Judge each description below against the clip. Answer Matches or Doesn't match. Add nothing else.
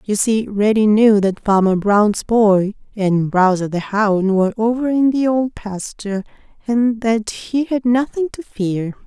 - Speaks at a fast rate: Doesn't match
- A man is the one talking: Doesn't match